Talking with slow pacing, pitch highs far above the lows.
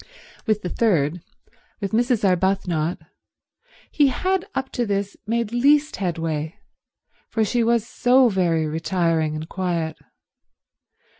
Yes: slow, 120 wpm; wide, 6.1 semitones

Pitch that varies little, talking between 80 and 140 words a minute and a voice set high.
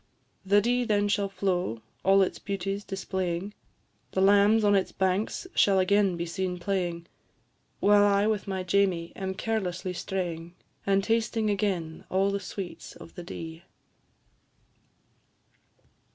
Yes: narrow, 2.1 semitones; slow, 135 wpm; high, 195 Hz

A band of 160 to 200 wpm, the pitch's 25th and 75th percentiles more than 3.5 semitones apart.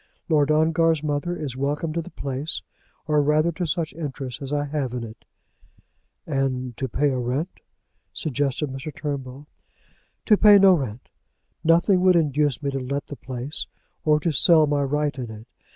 No: average, 170 wpm; average, 3.0 semitones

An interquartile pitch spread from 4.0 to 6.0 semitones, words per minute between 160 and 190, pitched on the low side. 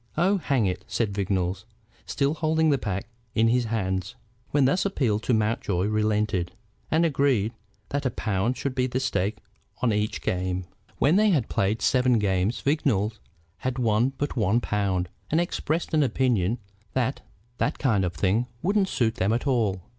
Yes: wide, 5.5 semitones; average, 165 wpm; low, 115 Hz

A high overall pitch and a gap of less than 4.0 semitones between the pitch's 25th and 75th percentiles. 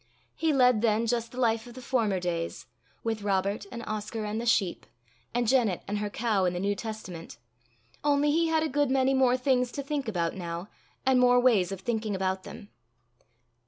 No: high, 225 Hz; average, 4.3 semitones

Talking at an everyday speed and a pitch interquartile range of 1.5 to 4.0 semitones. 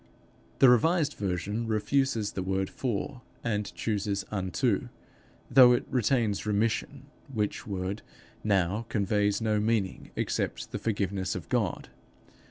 No: slow, 125 wpm; average, 2.9 semitones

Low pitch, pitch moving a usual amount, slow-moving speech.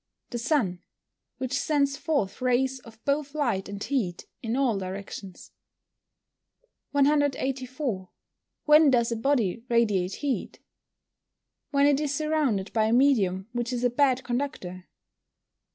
No: very high, 250 Hz; average, 5.0 semitones; slow, 130 wpm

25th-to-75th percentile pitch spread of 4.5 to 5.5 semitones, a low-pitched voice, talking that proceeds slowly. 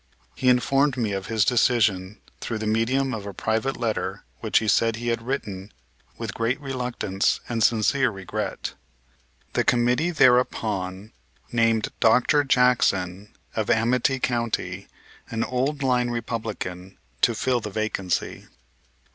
No: average, 2.9 semitones; low, 115 Hz; slow, 130 wpm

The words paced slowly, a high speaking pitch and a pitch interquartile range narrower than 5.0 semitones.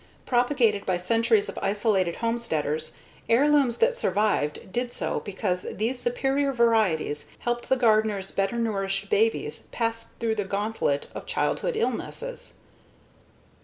Yes: slow, 125 wpm; high, 230 Hz; average, 4.0 semitones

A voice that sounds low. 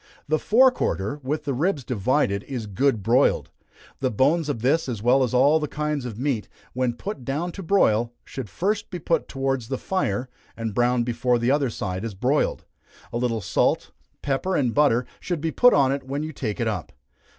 Yes: low, 130 Hz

